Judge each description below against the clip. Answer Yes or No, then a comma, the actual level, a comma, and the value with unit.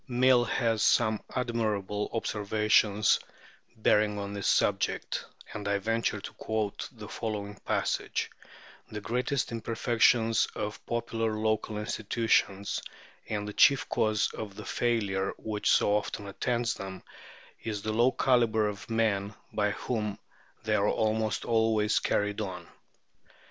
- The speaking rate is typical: No, slow, 130 wpm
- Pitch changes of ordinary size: No, narrow, 1.8 semitones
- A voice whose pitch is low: Yes, low, 110 Hz